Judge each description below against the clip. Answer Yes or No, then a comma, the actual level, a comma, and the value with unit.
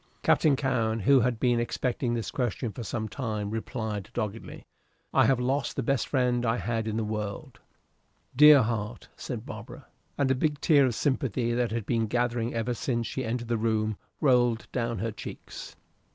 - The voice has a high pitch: No, low, 120 Hz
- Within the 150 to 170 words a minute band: No, average, 180 wpm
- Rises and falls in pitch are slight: Yes, narrow, 2.3 semitones